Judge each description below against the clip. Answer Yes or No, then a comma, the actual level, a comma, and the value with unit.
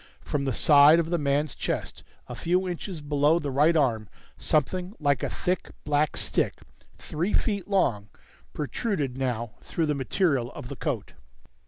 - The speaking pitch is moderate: Yes, medium, 150 Hz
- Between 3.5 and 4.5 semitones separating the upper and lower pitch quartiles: Yes, average, 4.0 semitones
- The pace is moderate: Yes, average, 160 wpm